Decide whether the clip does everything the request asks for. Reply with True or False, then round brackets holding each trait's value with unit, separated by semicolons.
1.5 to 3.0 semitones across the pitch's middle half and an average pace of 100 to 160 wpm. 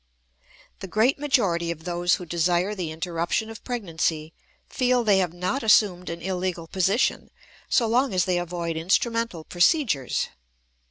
False (4.6 semitones; 150 wpm)